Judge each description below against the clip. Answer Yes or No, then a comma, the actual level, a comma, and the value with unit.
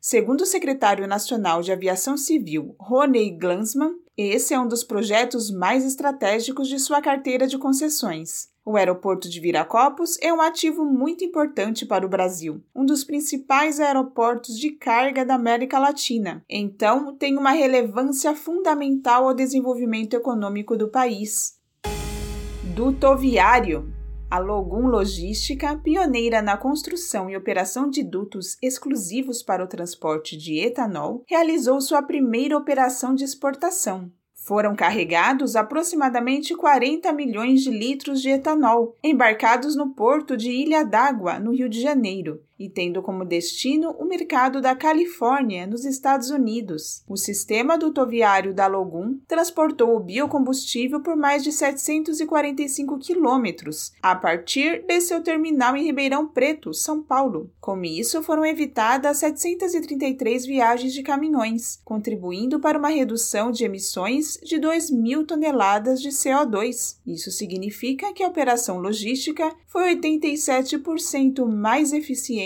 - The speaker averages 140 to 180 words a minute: No, average, 130 wpm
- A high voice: Yes, very high, 260 Hz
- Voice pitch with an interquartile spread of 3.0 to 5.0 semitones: No, wide, 5.5 semitones